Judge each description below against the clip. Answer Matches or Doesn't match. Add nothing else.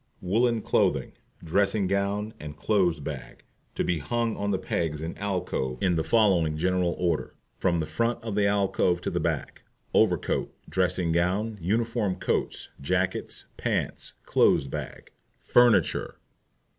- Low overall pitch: Matches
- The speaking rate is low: Doesn't match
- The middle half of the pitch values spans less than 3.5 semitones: Doesn't match